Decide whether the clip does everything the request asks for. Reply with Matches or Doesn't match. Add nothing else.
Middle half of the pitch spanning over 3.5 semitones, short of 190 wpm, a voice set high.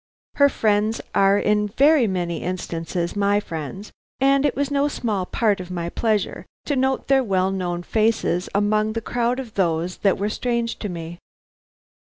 Matches